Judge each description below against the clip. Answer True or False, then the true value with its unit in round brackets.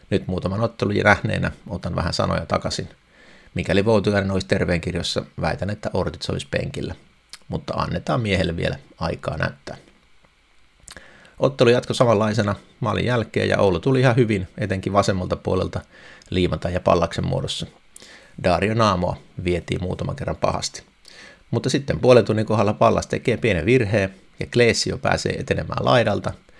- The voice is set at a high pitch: False (105 Hz)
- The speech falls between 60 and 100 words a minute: False (135 wpm)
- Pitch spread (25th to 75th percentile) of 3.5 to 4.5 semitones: True (4.1 semitones)